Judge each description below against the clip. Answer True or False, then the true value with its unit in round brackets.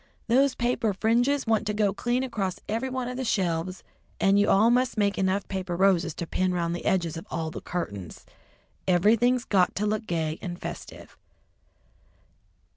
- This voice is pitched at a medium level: False (200 Hz)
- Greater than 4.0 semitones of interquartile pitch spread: True (4.8 semitones)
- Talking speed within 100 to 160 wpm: False (175 wpm)